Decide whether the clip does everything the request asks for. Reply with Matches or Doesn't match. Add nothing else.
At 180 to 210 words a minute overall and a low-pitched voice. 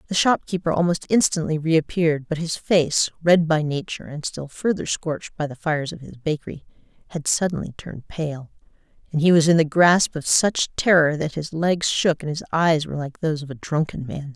Doesn't match